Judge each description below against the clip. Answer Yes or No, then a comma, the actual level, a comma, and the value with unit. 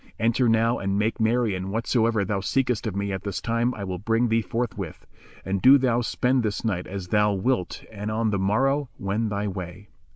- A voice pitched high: No, low, 110 Hz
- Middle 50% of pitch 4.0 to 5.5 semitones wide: No, average, 2.9 semitones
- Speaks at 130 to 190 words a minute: No, fast, 205 wpm